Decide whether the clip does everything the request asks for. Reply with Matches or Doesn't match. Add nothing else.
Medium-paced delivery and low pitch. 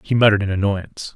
Doesn't match